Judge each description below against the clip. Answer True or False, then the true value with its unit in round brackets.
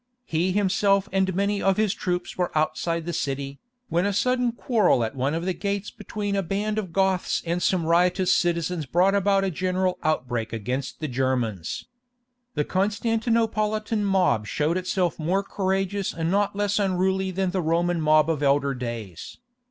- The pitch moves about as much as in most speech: True (4.2 semitones)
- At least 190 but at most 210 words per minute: False (165 wpm)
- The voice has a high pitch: False (180 Hz)